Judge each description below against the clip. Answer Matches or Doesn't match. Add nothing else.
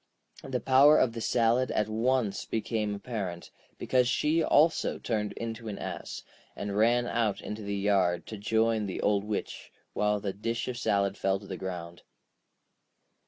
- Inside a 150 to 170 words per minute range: Matches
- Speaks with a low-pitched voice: Matches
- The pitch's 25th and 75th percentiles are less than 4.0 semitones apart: Matches